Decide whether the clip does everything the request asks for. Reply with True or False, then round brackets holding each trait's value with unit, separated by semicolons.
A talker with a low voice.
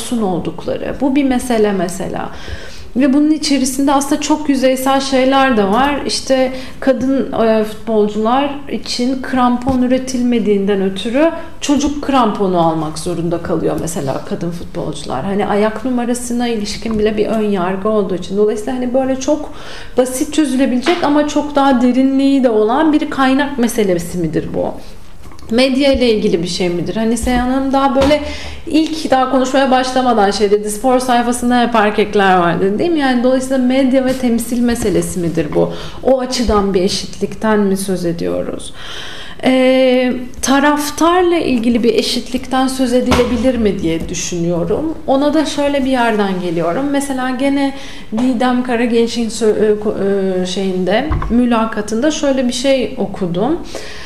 False (245 Hz)